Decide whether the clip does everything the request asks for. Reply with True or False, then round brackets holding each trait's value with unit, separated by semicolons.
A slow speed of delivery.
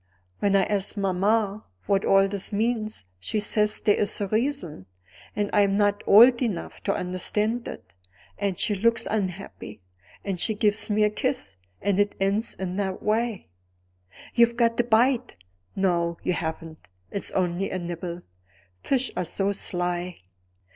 False (155 wpm)